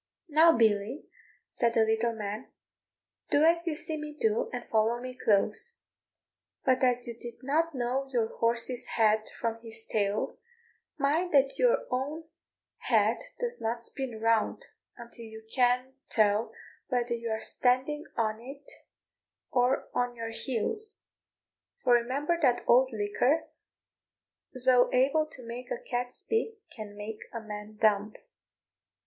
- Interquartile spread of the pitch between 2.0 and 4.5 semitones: Yes, average, 3.6 semitones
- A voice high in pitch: Yes, high, 245 Hz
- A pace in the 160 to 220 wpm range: No, average, 140 wpm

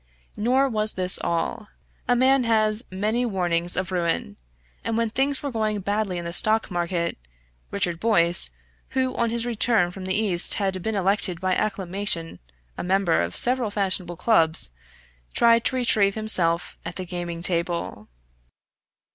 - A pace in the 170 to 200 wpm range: No, average, 155 wpm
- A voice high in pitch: Yes, high, 195 Hz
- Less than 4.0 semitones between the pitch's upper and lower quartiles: No, average, 4.3 semitones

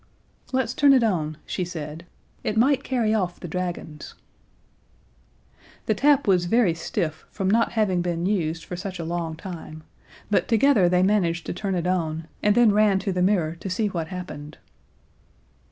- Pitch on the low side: No, medium, 180 Hz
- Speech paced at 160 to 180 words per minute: Yes, average, 170 wpm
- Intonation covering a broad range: No, average, 4.1 semitones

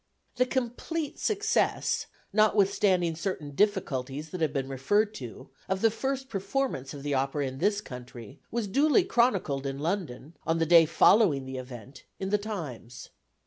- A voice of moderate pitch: Yes, medium, 170 Hz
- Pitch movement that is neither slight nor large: No, wide, 7.9 semitones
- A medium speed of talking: Yes, average, 155 wpm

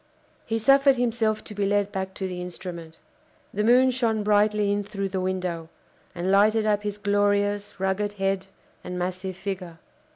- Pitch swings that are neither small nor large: No, narrow, 2.1 semitones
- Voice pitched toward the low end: No, high, 205 Hz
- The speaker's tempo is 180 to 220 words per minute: No, average, 165 wpm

